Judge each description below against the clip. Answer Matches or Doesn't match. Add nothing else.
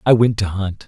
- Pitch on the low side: Matches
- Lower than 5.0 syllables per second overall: Doesn't match